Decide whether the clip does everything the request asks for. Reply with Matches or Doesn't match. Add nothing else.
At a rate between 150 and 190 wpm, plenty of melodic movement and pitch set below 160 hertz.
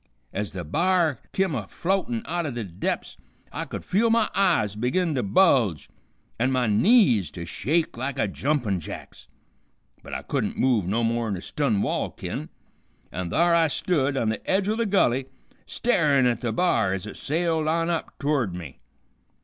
Matches